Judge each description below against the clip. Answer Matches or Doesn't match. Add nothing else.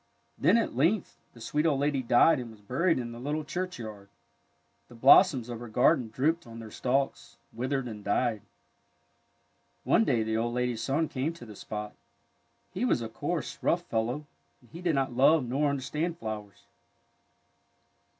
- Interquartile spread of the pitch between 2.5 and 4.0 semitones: Doesn't match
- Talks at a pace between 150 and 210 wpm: Matches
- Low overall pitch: Matches